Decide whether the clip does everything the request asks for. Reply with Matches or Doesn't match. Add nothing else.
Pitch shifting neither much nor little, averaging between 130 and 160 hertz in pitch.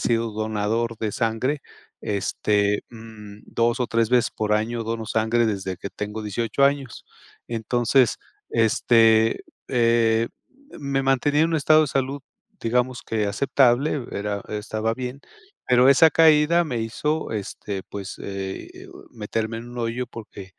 Doesn't match